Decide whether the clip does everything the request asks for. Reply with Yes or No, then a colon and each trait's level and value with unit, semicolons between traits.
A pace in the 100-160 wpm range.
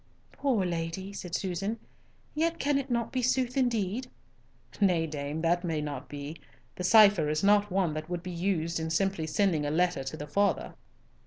No: average, 180 wpm